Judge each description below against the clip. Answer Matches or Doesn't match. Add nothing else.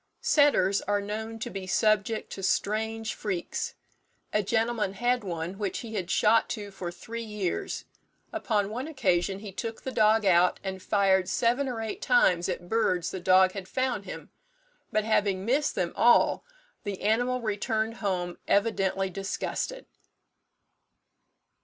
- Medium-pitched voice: Doesn't match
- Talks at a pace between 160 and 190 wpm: Doesn't match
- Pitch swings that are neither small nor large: Matches